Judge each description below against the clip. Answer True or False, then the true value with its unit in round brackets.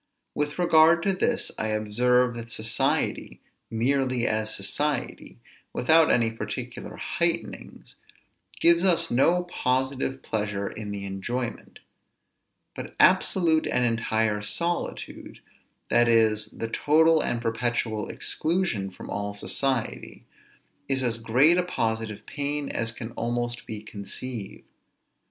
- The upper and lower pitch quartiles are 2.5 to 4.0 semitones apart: False (5.0 semitones)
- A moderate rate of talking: False (115 wpm)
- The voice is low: True (120 Hz)